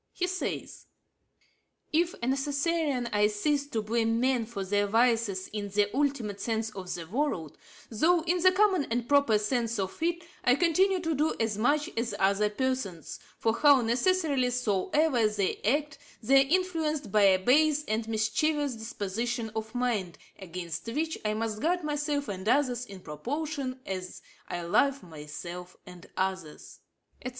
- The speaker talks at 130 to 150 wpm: No, average, 160 wpm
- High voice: Yes, high, 235 Hz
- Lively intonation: Yes, wide, 6.1 semitones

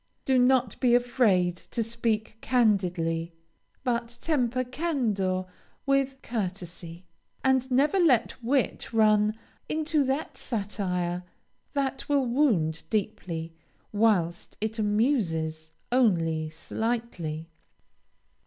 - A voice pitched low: No, high, 225 Hz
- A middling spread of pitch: No, wide, 6.2 semitones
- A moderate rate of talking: No, slow, 95 wpm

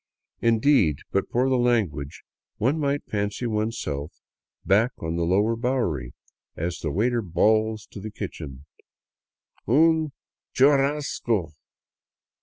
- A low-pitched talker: Yes, low, 110 Hz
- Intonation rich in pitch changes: Yes, wide, 6.7 semitones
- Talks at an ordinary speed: No, slow, 115 wpm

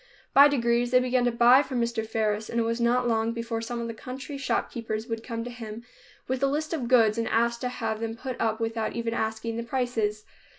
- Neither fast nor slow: No, fast, 230 wpm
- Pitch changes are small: Yes, narrow, 1.7 semitones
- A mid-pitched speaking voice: No, high, 235 Hz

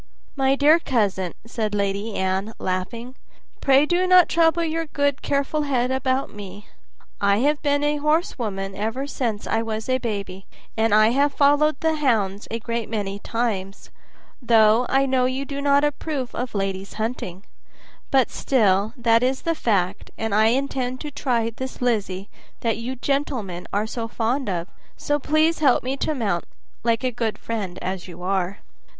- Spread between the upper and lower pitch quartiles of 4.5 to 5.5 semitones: Yes, average, 5.2 semitones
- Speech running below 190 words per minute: Yes, average, 170 wpm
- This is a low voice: No, high, 235 Hz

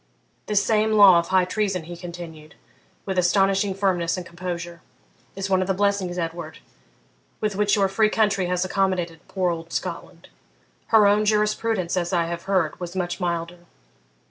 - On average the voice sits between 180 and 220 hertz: Yes, medium, 185 Hz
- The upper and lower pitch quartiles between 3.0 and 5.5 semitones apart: No, narrow, 2.6 semitones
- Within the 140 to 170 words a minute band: Yes, average, 165 wpm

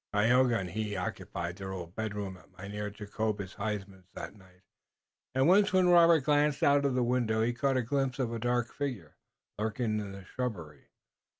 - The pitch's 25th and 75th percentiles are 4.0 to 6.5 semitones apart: Yes, average, 4.8 semitones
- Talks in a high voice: No, low, 110 Hz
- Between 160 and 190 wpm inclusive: Yes, average, 180 wpm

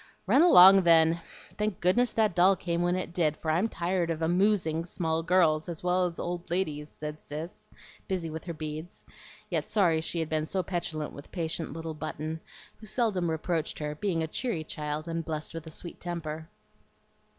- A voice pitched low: No, medium, 165 Hz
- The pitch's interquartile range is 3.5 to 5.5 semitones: No, narrow, 2.4 semitones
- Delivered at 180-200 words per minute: Yes, average, 185 wpm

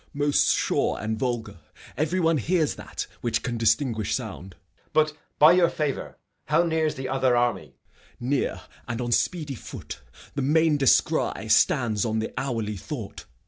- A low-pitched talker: Yes, low, 130 Hz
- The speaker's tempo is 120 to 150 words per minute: No, average, 165 wpm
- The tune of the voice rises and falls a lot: No, average, 5.0 semitones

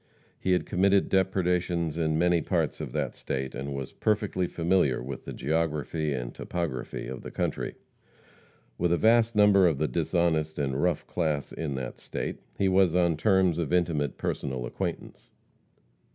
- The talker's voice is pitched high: No, very low, 85 Hz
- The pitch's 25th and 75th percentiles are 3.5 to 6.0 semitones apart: Yes, average, 3.9 semitones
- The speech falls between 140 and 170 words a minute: Yes, average, 160 wpm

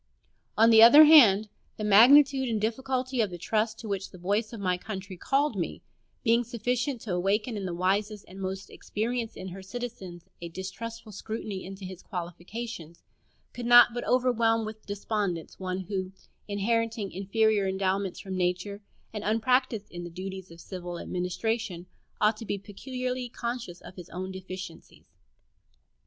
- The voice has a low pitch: No, high, 205 Hz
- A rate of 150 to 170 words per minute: Yes, average, 160 wpm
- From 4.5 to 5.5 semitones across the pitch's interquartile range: No, average, 3.6 semitones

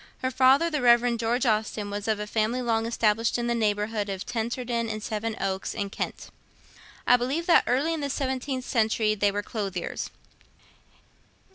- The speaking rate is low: No, average, 165 wpm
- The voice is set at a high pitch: Yes, high, 230 Hz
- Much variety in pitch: No, average, 2.9 semitones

